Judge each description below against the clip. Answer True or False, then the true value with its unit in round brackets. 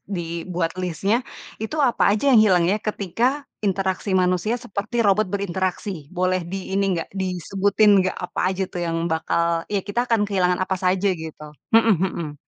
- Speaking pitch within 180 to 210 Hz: True (190 Hz)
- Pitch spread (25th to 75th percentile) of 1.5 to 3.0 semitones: True (2.4 semitones)